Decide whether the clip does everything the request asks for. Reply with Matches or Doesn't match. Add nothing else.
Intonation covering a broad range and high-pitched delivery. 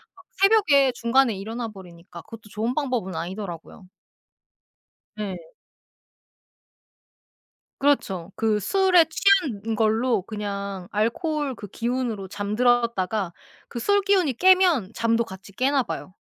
Matches